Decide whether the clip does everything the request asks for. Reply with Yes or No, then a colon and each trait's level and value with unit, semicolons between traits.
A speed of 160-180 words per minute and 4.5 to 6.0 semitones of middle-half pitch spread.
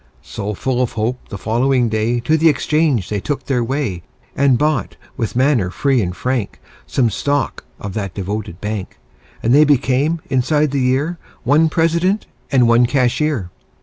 Yes: average, 165 wpm; average, 4.8 semitones